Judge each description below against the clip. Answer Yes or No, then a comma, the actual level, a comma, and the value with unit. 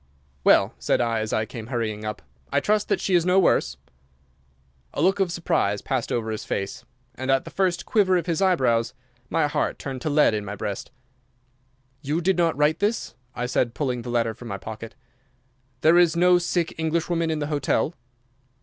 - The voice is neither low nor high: Yes, medium, 145 Hz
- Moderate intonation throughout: No, wide, 6.9 semitones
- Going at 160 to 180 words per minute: No, average, 195 wpm